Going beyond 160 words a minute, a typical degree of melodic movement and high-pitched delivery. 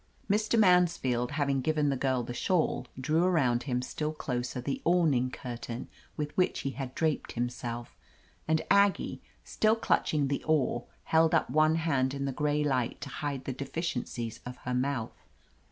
No: average, 170 wpm; average, 4.1 semitones; medium, 140 Hz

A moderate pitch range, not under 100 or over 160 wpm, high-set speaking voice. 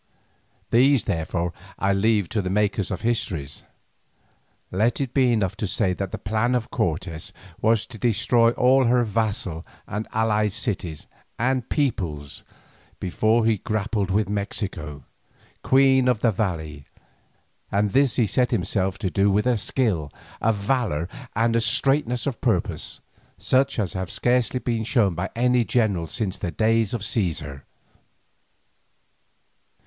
No: average, 4.1 semitones; average, 145 wpm; low, 110 Hz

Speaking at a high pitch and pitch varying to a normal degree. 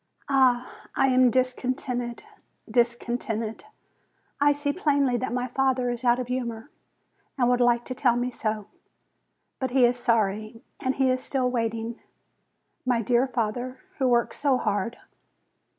No: high, 245 Hz; narrow, 1.6 semitones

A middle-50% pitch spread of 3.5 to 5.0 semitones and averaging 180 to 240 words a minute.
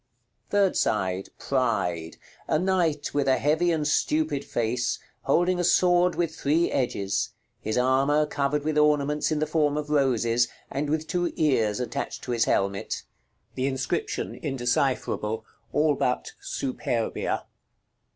No: average, 4.2 semitones; average, 140 wpm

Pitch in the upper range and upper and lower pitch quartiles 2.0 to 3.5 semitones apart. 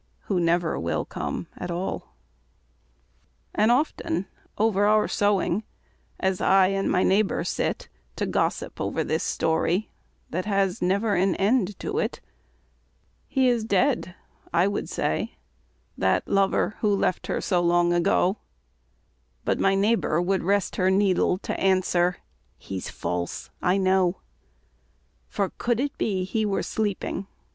Yes: high, 195 Hz; narrow, 2.6 semitones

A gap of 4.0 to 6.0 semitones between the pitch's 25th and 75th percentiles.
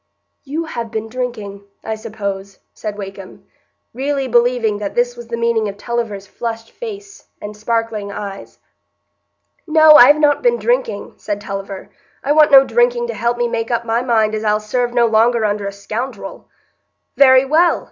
No: average, 3.3 semitones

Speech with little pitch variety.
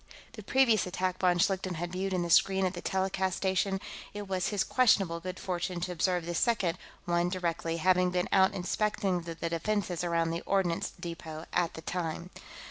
Yes: narrow, 1.9 semitones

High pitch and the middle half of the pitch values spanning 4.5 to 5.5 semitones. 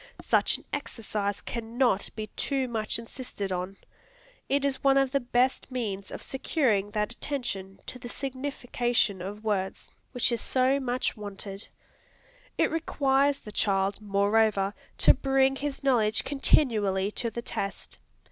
Yes: high, 235 Hz; average, 4.8 semitones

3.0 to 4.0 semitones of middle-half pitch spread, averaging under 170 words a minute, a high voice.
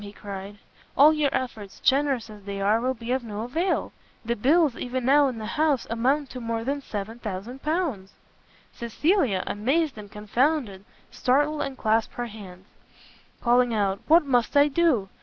No: average, 5.2 semitones; average, 160 wpm; high, 240 Hz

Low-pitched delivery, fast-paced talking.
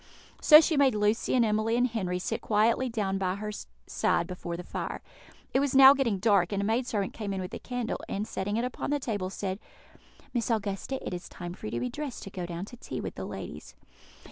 No: high, 210 Hz; fast, 235 wpm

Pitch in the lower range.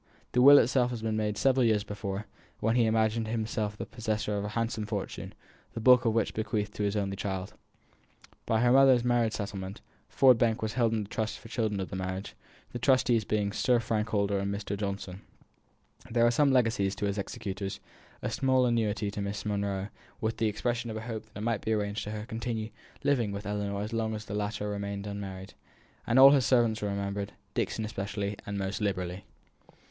Yes: low, 110 Hz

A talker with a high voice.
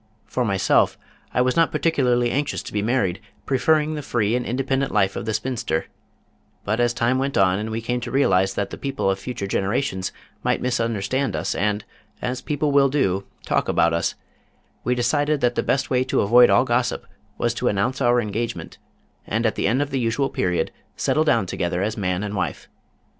No: low, 120 Hz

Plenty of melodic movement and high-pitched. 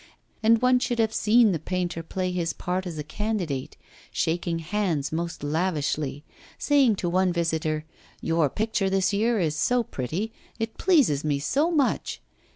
No: wide, 5.8 semitones; medium, 180 Hz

